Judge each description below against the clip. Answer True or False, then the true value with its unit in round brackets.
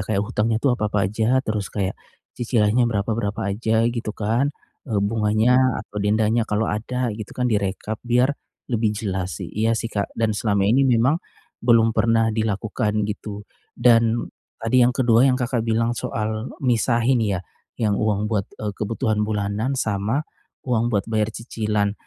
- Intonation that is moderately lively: False (2.1 semitones)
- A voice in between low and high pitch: False (110 Hz)